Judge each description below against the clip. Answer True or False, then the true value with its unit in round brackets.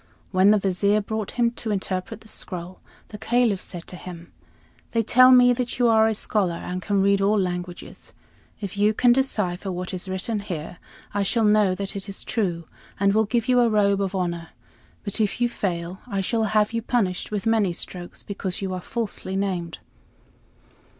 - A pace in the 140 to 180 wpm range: False (190 wpm)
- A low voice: False (200 Hz)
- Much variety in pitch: False (3.1 semitones)